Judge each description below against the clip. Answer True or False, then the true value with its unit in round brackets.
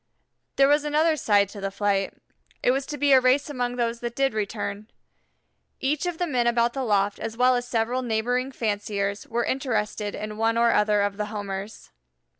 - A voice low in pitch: False (235 Hz)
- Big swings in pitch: False (3.7 semitones)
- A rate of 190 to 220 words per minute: True (195 wpm)